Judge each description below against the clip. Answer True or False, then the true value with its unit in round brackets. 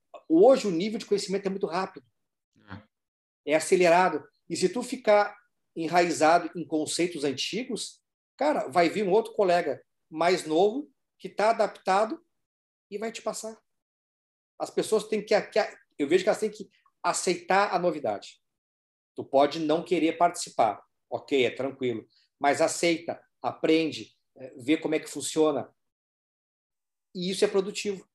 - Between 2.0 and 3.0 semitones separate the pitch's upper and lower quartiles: False (4.9 semitones)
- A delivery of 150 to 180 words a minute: False (140 wpm)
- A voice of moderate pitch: True (180 Hz)